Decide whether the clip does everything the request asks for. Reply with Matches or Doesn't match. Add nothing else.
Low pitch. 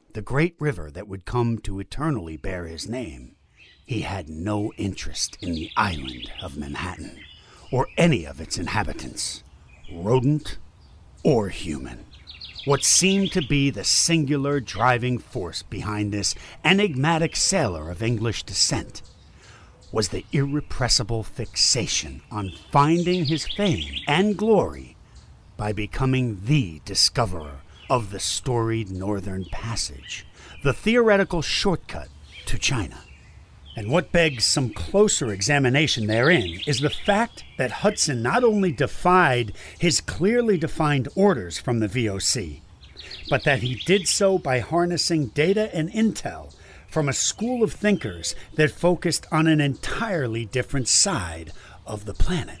Matches